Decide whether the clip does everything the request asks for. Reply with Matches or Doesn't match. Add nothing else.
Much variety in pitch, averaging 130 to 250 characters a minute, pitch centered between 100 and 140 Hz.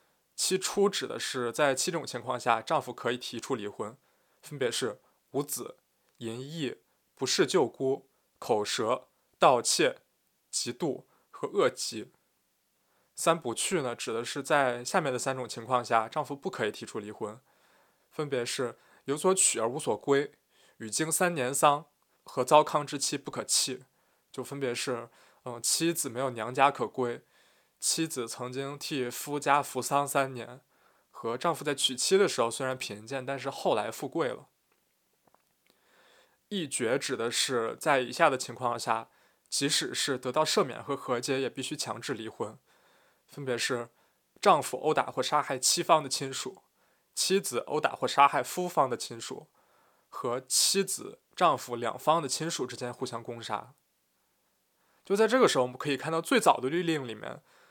Doesn't match